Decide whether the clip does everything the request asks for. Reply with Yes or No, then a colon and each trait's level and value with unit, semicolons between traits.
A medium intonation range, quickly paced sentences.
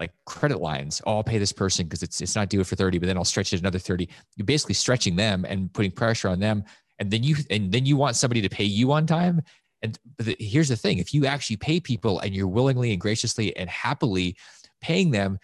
Yes: average, 4.7 semitones; fast, 240 wpm